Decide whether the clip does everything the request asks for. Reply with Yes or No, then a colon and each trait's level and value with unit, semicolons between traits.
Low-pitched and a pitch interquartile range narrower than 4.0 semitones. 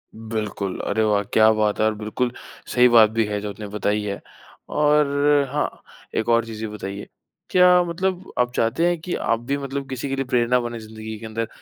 No: low, 115 Hz; average, 4.5 semitones